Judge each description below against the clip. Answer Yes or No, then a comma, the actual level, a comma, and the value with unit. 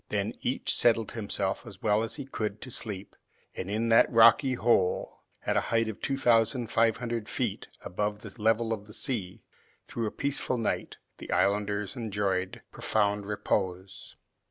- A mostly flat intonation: Yes, narrow, 2.3 semitones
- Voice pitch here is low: Yes, low, 110 Hz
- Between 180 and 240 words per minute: No, average, 165 wpm